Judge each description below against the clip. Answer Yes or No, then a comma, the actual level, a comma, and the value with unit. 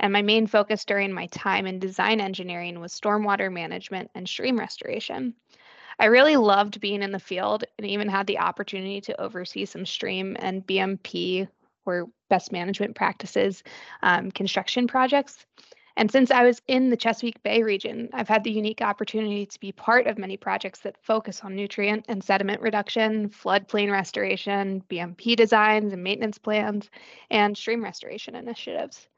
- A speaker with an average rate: Yes, average, 160 wpm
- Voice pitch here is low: No, high, 205 Hz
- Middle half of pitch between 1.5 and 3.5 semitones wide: Yes, narrow, 2.4 semitones